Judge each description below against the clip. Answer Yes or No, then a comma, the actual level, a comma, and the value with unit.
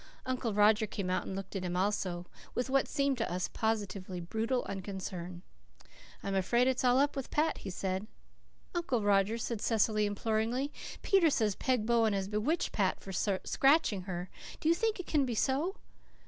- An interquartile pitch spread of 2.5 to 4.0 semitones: No, average, 5.1 semitones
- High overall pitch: Yes, high, 220 Hz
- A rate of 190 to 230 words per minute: No, average, 175 wpm